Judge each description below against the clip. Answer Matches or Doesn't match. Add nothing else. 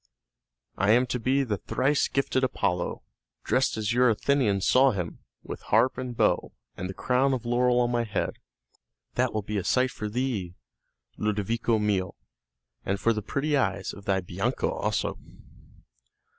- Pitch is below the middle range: Matches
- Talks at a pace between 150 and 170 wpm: Matches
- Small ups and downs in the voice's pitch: Doesn't match